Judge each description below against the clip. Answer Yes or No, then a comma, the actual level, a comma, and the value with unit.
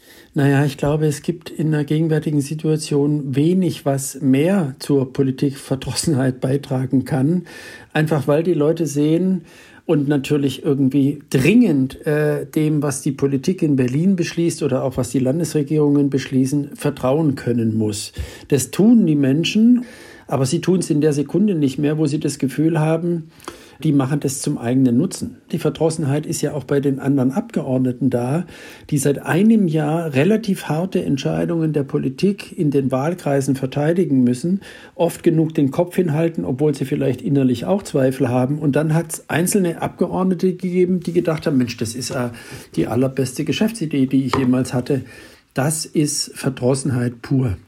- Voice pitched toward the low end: No, medium, 145 Hz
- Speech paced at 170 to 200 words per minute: No, average, 160 wpm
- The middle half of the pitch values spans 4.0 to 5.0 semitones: No, average, 3.4 semitones